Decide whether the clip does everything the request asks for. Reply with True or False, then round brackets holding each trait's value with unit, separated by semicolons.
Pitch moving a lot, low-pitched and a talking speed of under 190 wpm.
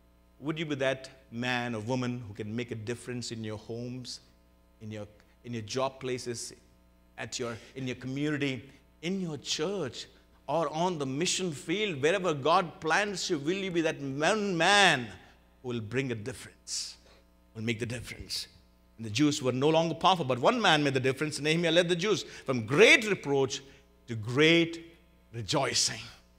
True (5.9 semitones; 125 Hz; 175 wpm)